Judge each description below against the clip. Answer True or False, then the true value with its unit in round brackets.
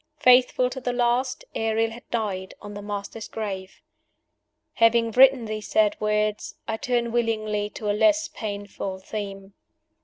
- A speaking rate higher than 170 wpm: False (145 wpm)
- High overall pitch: True (220 Hz)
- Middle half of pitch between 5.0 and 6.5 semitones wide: False (2.9 semitones)